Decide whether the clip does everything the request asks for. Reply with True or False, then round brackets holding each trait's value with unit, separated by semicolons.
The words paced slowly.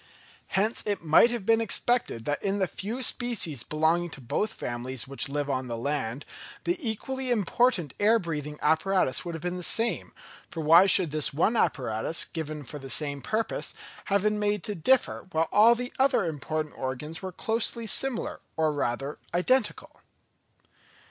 False (170 wpm)